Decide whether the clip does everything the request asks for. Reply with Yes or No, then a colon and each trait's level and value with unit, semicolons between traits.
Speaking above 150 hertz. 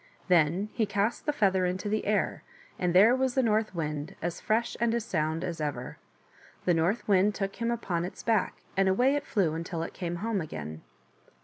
Yes: high, 190 Hz